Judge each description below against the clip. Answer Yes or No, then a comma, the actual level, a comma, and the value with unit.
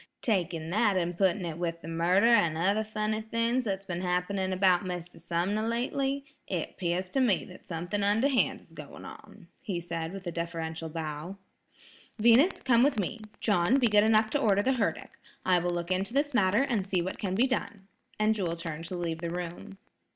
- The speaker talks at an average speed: Yes, average, 195 wpm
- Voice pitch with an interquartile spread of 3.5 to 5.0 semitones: Yes, average, 4.2 semitones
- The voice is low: No, high, 190 Hz